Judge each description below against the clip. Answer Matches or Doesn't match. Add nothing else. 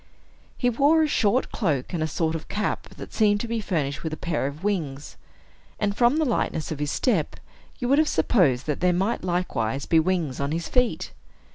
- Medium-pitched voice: Matches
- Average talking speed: Doesn't match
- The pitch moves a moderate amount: Doesn't match